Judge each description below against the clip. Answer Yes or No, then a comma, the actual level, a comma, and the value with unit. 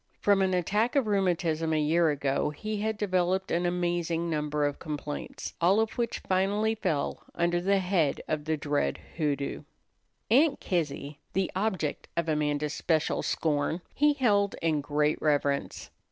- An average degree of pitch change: Yes, average, 4.6 semitones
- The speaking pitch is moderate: Yes, medium, 170 Hz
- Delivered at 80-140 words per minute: No, average, 155 wpm